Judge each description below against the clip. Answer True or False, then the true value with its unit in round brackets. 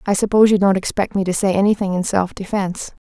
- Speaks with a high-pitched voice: True (195 Hz)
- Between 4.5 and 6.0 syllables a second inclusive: False (6.6 syllables/s)